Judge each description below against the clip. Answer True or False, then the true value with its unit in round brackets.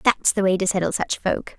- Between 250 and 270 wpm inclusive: True (265 wpm)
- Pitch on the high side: True (195 Hz)